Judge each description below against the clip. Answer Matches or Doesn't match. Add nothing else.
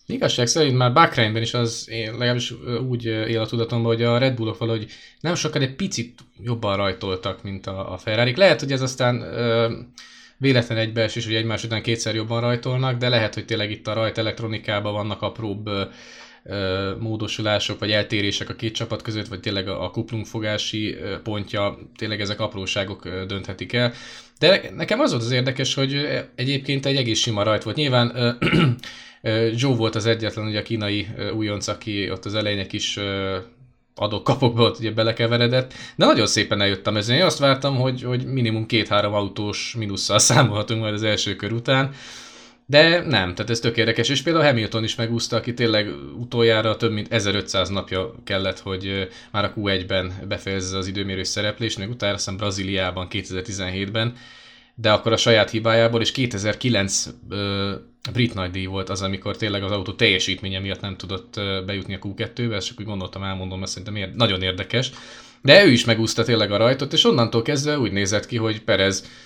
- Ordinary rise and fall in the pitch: Matches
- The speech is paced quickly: Matches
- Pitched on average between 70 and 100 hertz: Doesn't match